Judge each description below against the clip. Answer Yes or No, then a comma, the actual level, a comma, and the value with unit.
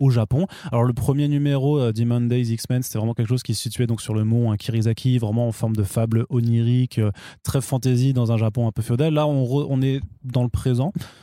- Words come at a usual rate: No, fast, 235 wpm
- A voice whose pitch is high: No, low, 120 Hz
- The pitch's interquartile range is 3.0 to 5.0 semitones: No, narrow, 2.6 semitones